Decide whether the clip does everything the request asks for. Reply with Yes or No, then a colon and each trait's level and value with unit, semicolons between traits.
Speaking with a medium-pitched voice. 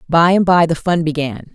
Yes: medium, 165 Hz